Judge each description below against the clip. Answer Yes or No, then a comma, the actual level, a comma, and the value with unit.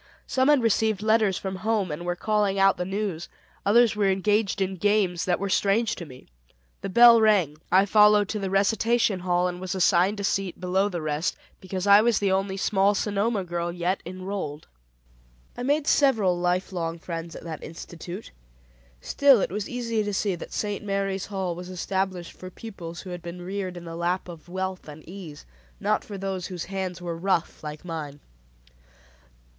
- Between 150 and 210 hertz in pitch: Yes, high, 190 Hz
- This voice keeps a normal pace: Yes, average, 185 wpm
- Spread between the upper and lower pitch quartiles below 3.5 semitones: Yes, average, 2.8 semitones